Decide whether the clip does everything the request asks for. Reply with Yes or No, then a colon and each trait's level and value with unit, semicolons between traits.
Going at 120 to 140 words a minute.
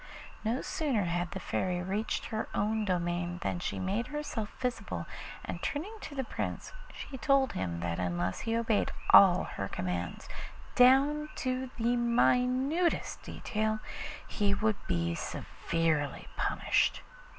Yes: slow, 135 wpm